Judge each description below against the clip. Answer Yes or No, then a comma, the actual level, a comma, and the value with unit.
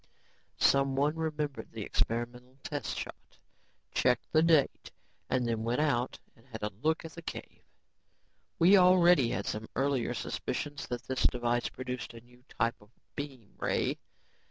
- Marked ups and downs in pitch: No, average, 4.0 semitones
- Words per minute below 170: Yes, average, 150 wpm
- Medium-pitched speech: No, low, 130 Hz